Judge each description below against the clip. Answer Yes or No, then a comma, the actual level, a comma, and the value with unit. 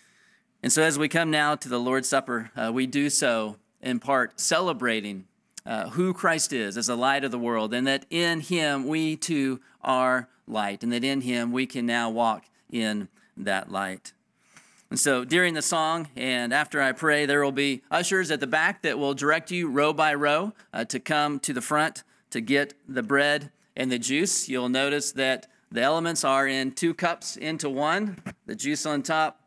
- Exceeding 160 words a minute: Yes, average, 200 wpm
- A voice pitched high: No, medium, 140 Hz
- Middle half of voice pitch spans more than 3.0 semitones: Yes, average, 3.9 semitones